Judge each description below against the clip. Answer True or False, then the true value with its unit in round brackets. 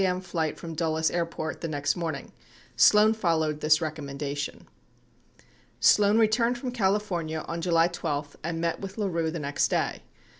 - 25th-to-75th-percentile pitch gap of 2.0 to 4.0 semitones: True (3.5 semitones)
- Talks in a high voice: False (165 Hz)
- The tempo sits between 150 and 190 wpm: True (160 wpm)